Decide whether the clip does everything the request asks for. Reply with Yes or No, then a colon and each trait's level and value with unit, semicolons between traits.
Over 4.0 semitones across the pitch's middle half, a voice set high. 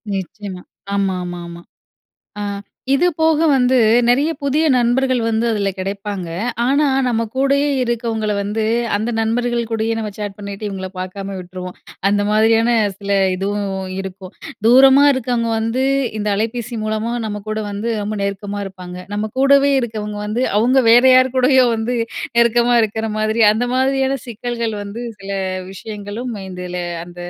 No: average, 3.4 semitones; high, 220 Hz